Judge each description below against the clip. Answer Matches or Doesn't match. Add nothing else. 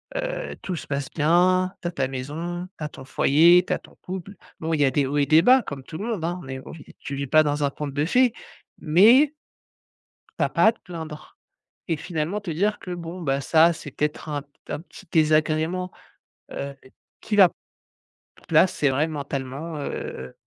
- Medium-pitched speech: Matches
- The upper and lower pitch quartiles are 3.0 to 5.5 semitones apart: Matches